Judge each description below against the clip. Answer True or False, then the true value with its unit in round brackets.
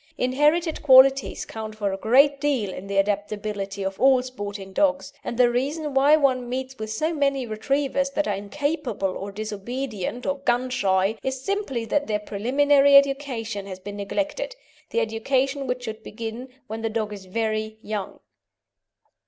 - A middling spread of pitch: True (4.8 semitones)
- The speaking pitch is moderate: False (245 Hz)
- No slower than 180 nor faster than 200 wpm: False (160 wpm)